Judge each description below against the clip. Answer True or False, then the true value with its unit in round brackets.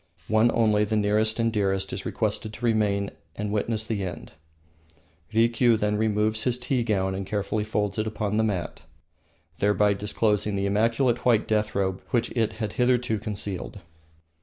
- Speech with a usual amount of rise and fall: False (1.7 semitones)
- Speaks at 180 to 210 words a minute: False (160 wpm)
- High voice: False (105 Hz)